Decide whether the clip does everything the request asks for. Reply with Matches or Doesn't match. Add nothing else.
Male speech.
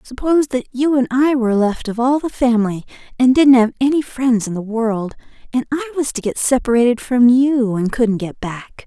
Doesn't match